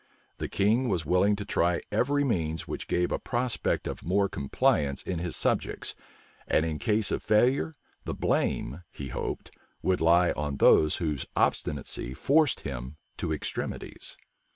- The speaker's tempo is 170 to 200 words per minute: No, average, 155 wpm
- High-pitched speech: No, very low, 90 Hz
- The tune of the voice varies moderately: No, wide, 6.0 semitones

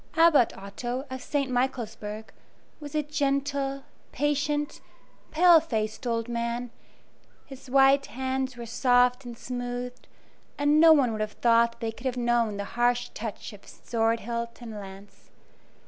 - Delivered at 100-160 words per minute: Yes, average, 145 wpm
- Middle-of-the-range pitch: No, high, 245 Hz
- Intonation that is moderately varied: Yes, average, 3.0 semitones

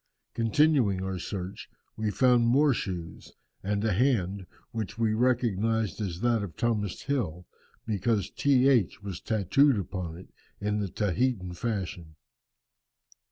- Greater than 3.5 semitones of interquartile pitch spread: Yes, average, 4.1 semitones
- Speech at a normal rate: No, slow, 130 wpm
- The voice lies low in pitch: Yes, low, 105 Hz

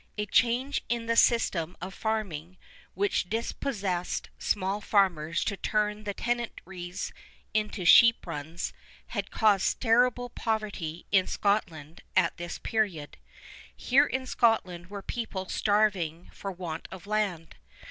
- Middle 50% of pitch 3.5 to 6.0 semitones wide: Yes, average, 4.1 semitones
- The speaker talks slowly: Yes, slow, 125 wpm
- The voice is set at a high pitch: Yes, high, 200 Hz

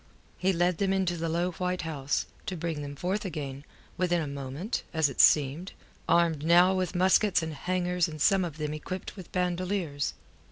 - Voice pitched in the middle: Yes, medium, 170 Hz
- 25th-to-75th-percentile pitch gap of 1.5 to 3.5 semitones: Yes, average, 3.2 semitones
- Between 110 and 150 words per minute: No, average, 185 wpm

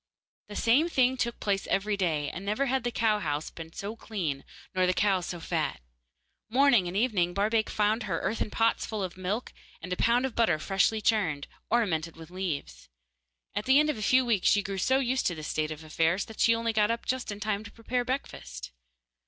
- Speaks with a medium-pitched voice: No, high, 205 Hz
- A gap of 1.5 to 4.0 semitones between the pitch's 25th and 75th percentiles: No, average, 4.8 semitones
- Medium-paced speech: No, fast, 215 wpm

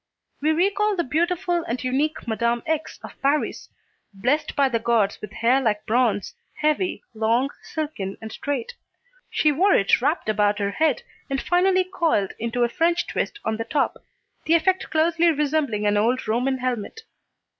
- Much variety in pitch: Yes, wide, 6.1 semitones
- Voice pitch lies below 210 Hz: No, very high, 270 Hz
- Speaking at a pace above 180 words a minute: No, average, 165 wpm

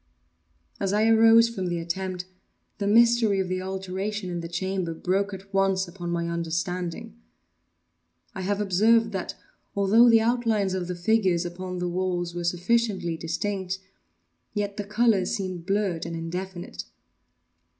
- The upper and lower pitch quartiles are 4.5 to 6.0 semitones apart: No, average, 2.9 semitones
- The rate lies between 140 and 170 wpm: Yes, average, 145 wpm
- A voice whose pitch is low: No, high, 190 Hz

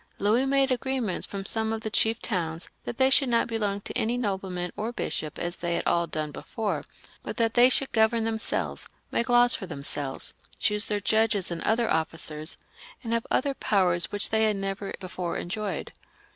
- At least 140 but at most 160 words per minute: No, average, 185 wpm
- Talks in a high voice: Yes, high, 210 Hz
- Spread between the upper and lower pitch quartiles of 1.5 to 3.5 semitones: No, average, 4.6 semitones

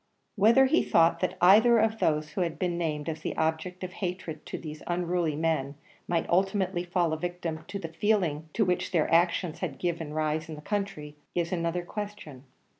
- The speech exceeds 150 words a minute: Yes, average, 190 wpm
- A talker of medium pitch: Yes, medium, 175 Hz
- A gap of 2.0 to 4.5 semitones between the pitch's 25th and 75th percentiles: Yes, average, 3.0 semitones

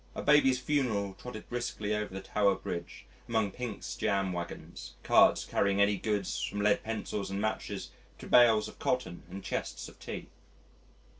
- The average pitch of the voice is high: No, low, 105 Hz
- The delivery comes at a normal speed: Yes, average, 160 wpm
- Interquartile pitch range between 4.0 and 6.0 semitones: No, average, 3.1 semitones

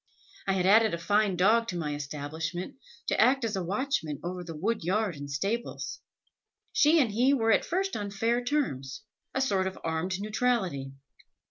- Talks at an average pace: Yes, average, 175 wpm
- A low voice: No, high, 195 Hz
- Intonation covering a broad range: Yes, wide, 5.9 semitones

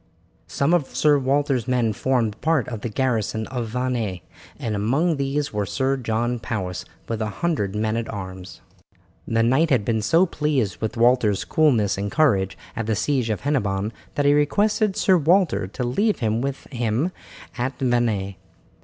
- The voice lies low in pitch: Yes, low, 120 Hz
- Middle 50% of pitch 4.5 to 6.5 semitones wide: Yes, average, 4.8 semitones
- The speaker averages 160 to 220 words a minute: Yes, average, 170 wpm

